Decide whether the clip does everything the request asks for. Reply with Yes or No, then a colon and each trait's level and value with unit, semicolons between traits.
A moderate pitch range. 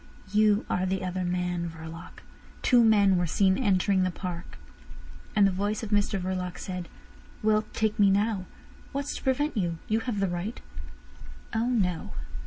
Yes: average, 3.0 semitones